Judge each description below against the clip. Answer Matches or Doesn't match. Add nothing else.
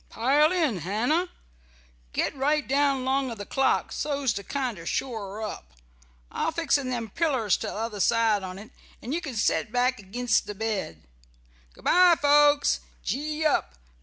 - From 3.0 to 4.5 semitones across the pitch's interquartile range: Doesn't match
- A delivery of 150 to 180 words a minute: Matches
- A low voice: Doesn't match